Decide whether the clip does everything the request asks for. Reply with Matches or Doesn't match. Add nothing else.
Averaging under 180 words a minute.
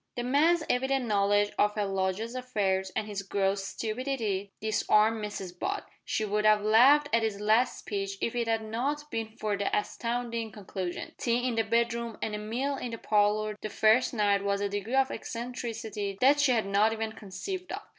Doesn't match